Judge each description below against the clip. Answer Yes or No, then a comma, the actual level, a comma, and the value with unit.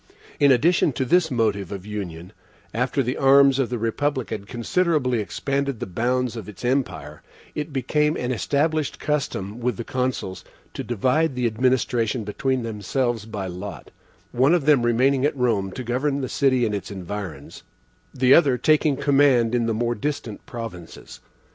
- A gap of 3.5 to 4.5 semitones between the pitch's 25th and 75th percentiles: Yes, average, 4.2 semitones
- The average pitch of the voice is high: No, low, 125 Hz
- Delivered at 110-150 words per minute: No, average, 165 wpm